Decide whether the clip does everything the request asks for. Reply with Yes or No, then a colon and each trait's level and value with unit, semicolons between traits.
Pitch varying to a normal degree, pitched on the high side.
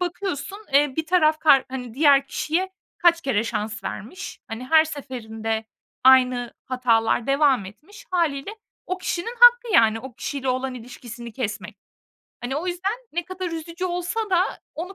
No: wide, 6.2 semitones; very high, 280 Hz